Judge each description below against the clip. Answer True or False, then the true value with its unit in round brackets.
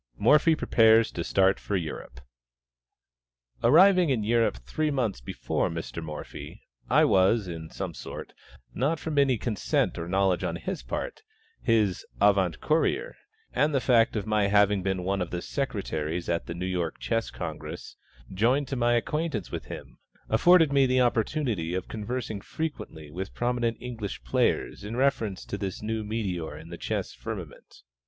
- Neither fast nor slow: True (160 wpm)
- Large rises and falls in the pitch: True (5.7 semitones)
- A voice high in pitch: False (105 Hz)